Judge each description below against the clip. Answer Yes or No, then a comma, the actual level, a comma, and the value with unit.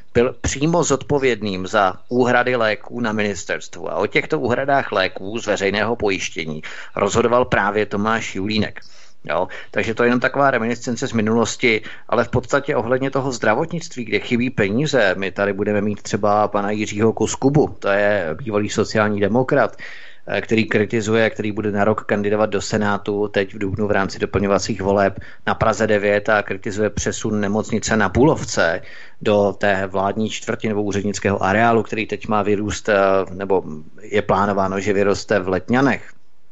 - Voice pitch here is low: Yes, low, 105 Hz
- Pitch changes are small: Yes, narrow, 2.3 semitones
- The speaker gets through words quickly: No, average, 155 wpm